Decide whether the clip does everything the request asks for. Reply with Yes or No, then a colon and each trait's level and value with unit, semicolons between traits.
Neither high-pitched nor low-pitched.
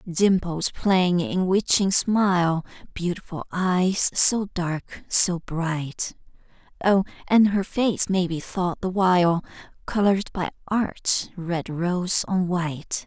Yes: medium, 180 Hz